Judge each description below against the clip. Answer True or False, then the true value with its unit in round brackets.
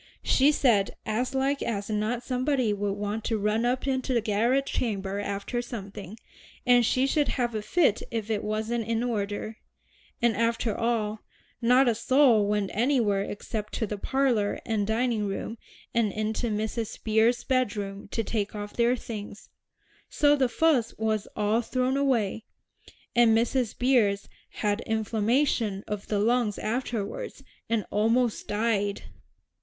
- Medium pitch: False (225 Hz)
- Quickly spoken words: False (150 wpm)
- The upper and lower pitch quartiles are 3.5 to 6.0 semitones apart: False (2.9 semitones)